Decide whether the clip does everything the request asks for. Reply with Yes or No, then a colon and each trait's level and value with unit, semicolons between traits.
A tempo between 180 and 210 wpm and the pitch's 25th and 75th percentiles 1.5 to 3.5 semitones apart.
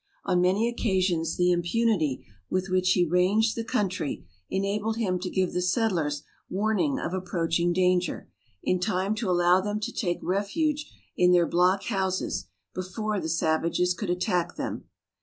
No: average, 155 wpm; average, 2.8 semitones